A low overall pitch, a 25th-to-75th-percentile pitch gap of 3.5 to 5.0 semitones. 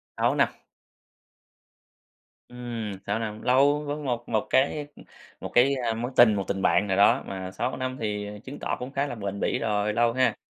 Yes: low, 115 Hz; average, 3.8 semitones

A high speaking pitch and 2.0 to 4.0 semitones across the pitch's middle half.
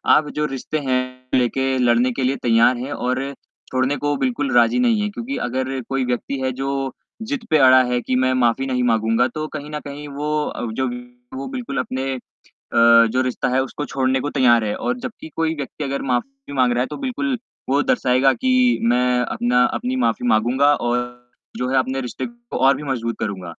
No: low, 130 Hz; average, 2.8 semitones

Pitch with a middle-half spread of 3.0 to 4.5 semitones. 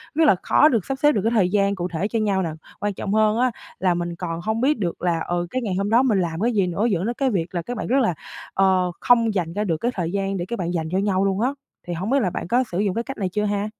Yes: average, 4.2 semitones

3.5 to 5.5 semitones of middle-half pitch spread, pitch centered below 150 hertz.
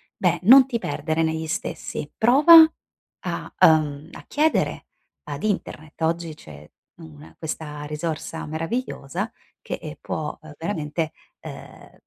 No: average, 4.8 semitones; medium, 160 Hz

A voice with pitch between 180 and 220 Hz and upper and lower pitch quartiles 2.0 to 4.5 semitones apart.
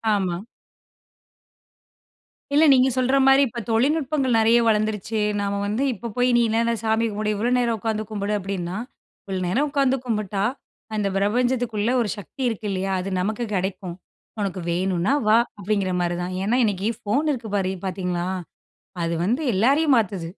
Yes: high, 215 Hz; average, 4.1 semitones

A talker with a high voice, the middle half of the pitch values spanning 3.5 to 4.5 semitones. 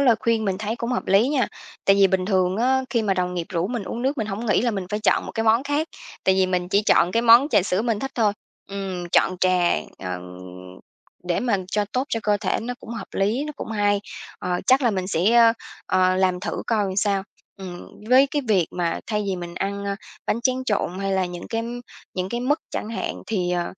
Yes: high, 205 Hz; average, 4.0 semitones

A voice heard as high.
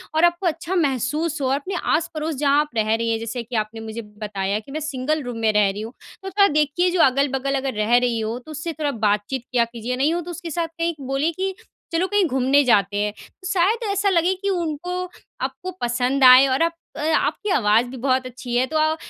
Yes: very high, 275 Hz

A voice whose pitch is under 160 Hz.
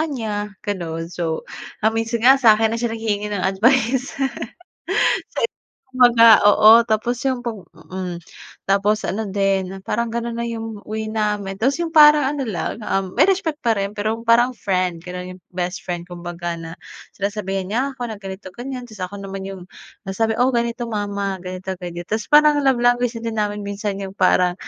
No: high, 210 Hz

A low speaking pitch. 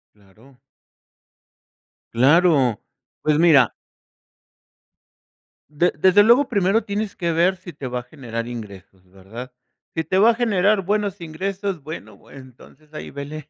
No: medium, 155 Hz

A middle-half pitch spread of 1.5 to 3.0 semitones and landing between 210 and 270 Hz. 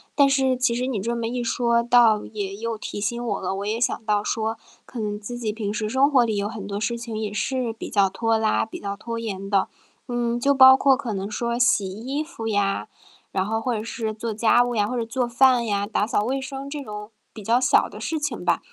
Yes: narrow, 2.6 semitones; high, 230 Hz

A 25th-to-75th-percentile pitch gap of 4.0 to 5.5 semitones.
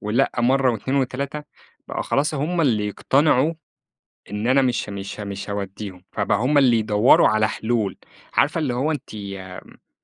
Yes: average, 5.0 semitones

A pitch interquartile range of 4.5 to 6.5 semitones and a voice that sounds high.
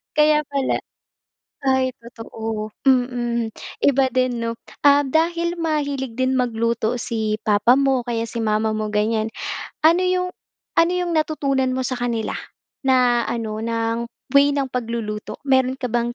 No: average, 3.4 semitones; very high, 250 Hz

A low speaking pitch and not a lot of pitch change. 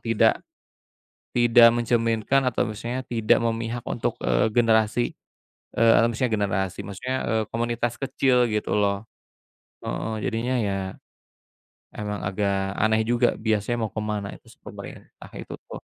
Yes: low, 115 Hz; narrow, 2.1 semitones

